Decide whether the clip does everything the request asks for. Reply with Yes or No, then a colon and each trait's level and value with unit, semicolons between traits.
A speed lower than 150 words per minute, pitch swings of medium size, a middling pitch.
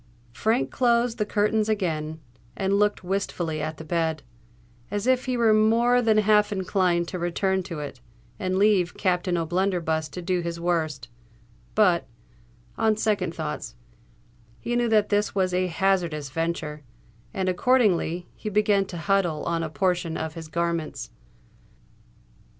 Yes: average, 140 wpm; average, 4.5 semitones; medium, 180 Hz